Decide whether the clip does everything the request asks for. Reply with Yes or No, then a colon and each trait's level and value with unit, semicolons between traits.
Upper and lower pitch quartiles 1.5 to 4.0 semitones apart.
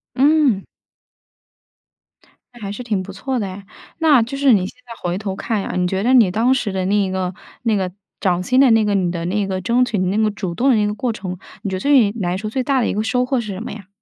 No: average, 4.6 semitones